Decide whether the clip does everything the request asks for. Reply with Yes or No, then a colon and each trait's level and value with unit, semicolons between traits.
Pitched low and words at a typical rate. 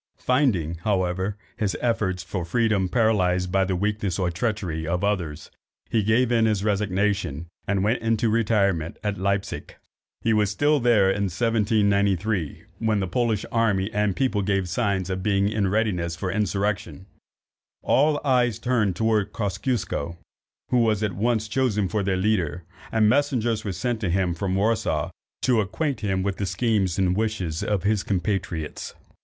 Yes: low, 100 Hz; average, 160 wpm